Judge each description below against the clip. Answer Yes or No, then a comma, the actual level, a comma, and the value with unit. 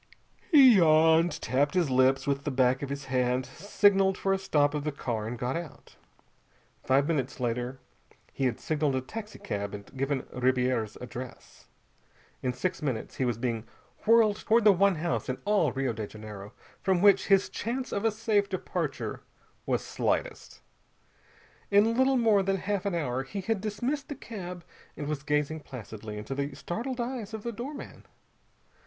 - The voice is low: No, medium, 155 Hz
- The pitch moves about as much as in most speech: No, wide, 7.9 semitones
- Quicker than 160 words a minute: Yes, average, 170 wpm